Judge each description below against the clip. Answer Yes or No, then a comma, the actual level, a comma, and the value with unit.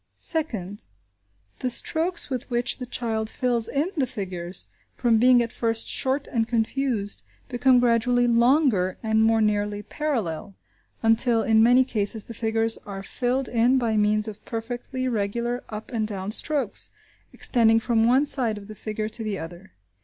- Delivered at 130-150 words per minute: No, average, 160 wpm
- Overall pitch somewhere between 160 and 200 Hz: No, high, 230 Hz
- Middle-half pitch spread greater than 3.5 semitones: No, average, 2.7 semitones